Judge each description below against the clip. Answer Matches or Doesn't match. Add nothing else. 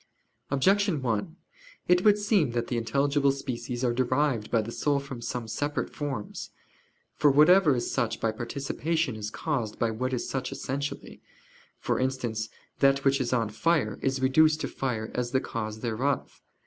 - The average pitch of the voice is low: Matches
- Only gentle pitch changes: Doesn't match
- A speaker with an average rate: Matches